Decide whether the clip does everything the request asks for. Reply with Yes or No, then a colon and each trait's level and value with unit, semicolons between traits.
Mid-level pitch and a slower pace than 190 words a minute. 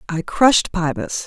Yes: medium, 180 Hz; average, 140 wpm